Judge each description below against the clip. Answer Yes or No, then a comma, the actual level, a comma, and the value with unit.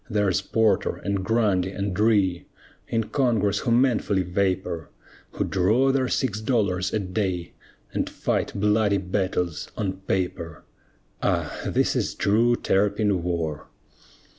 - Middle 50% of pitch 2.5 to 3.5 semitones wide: Yes, average, 3.1 semitones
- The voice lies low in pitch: Yes, low, 100 Hz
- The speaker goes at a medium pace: No, slow, 125 wpm